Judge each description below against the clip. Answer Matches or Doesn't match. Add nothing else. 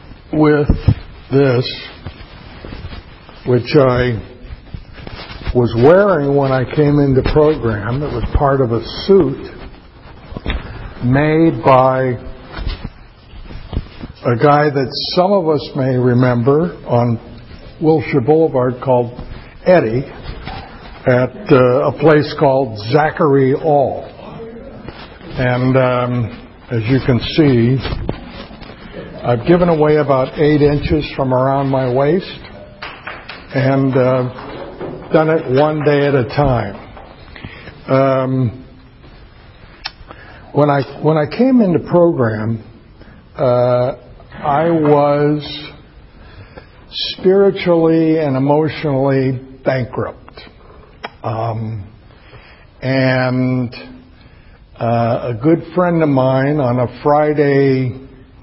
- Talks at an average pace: Doesn't match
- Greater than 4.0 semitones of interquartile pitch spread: Doesn't match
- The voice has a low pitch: Matches